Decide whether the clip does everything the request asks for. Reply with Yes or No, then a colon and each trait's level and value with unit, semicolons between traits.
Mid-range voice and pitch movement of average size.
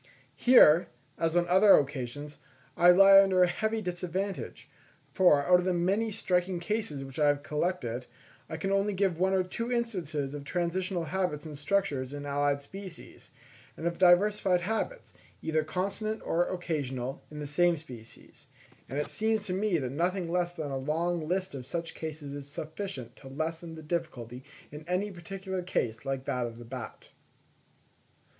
Yes: medium, 170 Hz; average, 4.7 semitones